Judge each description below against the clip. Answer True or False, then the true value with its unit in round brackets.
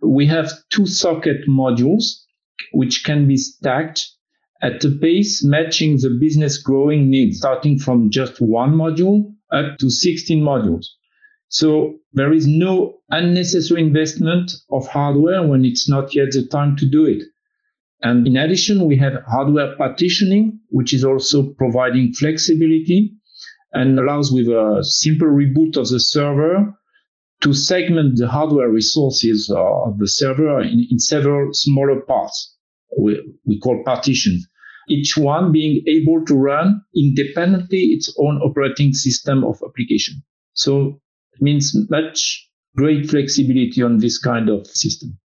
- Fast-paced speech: False (140 wpm)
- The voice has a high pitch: False (145 Hz)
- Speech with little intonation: False (3.5 semitones)